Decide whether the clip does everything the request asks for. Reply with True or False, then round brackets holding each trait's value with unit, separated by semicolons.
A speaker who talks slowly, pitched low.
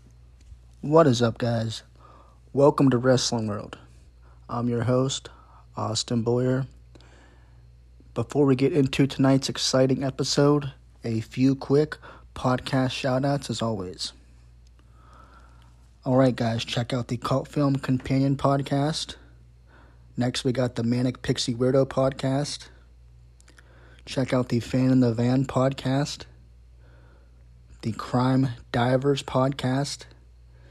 True (115 wpm; 120 Hz)